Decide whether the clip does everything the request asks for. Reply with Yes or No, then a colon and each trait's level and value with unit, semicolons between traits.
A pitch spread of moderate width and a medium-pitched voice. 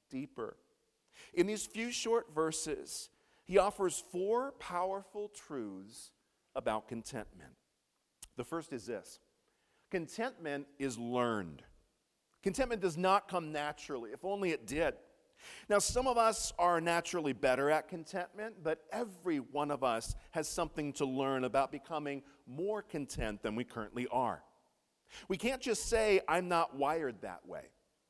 No: wide, 7.2 semitones; medium, 170 Hz